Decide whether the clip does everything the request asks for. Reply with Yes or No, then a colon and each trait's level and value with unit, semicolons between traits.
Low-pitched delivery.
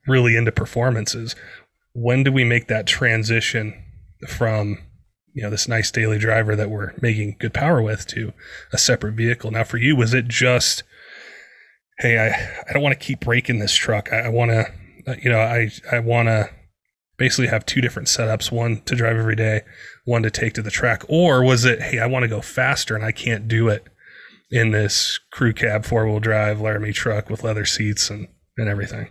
Yes: low, 115 Hz